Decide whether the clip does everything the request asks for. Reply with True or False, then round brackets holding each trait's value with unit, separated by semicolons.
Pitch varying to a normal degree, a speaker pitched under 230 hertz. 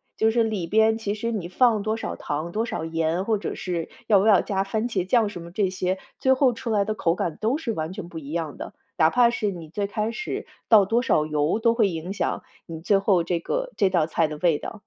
True (4.7 semitones; 200 Hz)